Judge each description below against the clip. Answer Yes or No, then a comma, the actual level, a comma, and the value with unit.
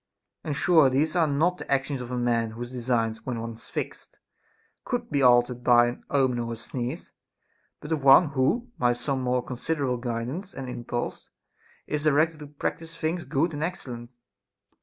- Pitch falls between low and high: No, low, 130 Hz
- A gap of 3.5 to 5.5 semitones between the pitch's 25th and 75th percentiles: Yes, average, 4.0 semitones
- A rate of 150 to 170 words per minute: No, average, 180 wpm